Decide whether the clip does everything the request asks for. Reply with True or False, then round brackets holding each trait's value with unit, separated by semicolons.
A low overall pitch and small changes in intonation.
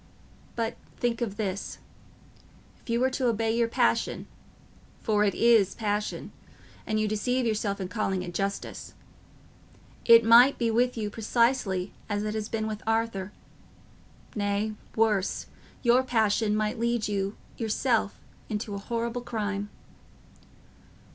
False (220 Hz; 2.3 semitones)